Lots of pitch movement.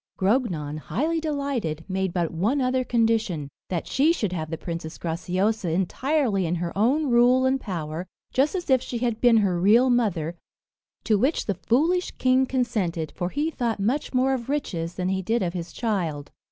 Yes: wide, 6.8 semitones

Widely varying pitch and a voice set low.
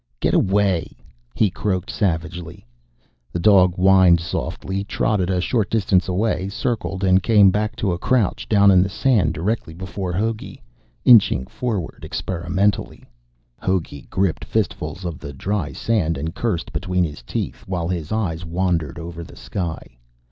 No: average, 3.1 semitones; very low, 95 Hz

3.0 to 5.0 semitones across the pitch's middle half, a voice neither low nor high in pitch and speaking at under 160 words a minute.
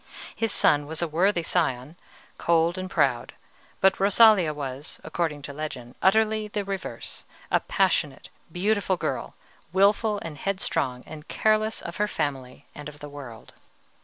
No: wide, 5.5 semitones; medium, 170 Hz; average, 140 wpm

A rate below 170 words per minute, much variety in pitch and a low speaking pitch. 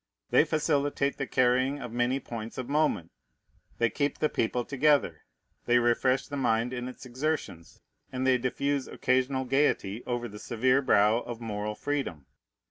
No: average, 155 wpm; average, 3.0 semitones; low, 125 Hz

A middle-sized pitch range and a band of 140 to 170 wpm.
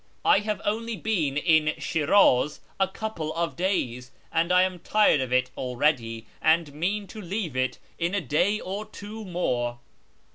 No: wide, 6.2 semitones; average, 160 wpm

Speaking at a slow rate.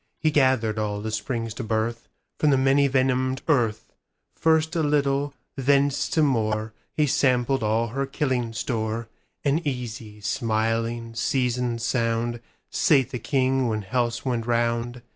Yes: slow, 125 wpm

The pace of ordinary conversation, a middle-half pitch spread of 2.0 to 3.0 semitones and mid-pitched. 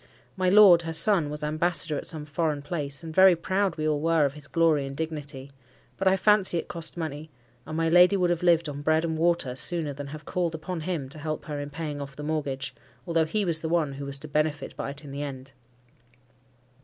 No: fast, 230 wpm; average, 2.7 semitones; medium, 155 Hz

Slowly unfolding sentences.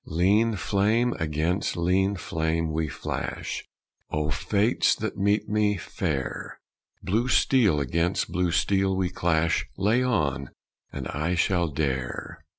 Yes: slow, 125 wpm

